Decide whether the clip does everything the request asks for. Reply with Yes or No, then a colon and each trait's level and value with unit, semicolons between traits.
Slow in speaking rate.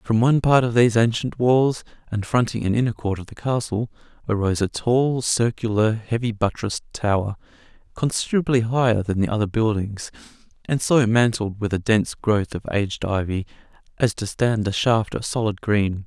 No: average, 170 wpm